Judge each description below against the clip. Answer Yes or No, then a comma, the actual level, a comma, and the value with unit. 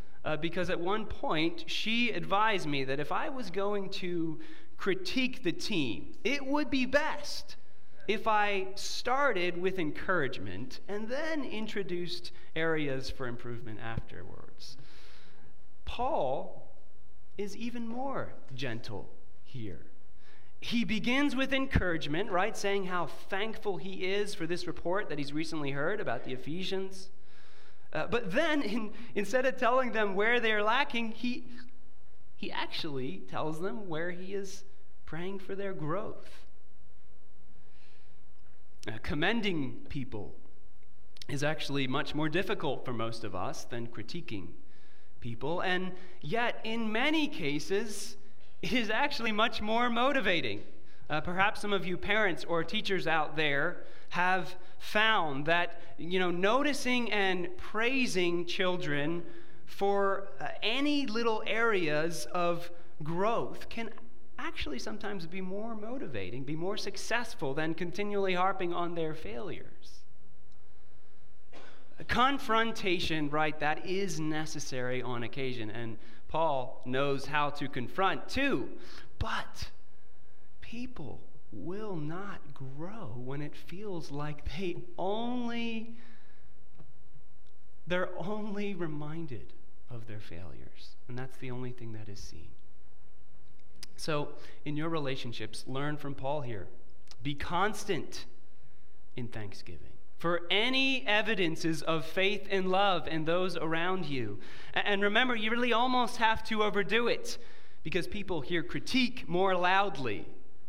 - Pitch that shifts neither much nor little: No, wide, 6.7 semitones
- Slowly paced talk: Yes, slow, 125 wpm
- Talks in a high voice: No, medium, 180 Hz